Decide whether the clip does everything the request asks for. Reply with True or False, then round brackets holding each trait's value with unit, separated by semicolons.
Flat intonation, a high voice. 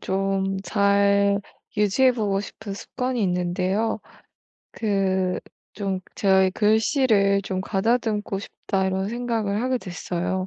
True (2.3 semitones; 200 Hz)